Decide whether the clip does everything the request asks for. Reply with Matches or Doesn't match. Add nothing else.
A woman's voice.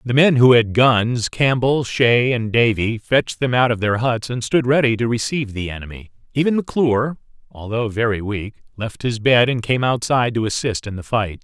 Doesn't match